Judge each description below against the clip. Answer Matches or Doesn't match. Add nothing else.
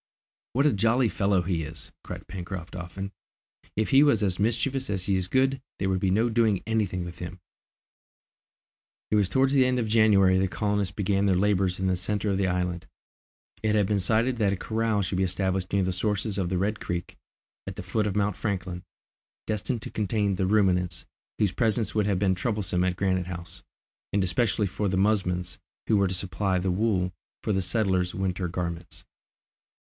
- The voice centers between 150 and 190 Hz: Doesn't match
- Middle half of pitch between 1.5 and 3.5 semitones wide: Matches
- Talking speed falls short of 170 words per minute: Doesn't match